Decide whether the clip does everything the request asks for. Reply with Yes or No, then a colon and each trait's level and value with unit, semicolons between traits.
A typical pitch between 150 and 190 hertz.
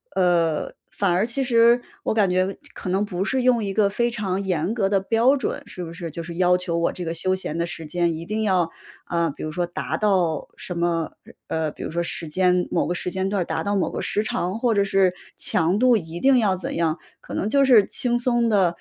Yes: medium, 185 Hz